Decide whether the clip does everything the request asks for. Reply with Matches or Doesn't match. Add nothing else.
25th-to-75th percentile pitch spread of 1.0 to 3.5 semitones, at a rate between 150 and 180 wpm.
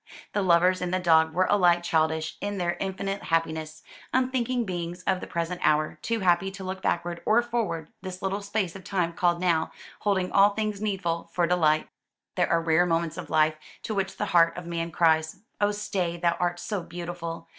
Doesn't match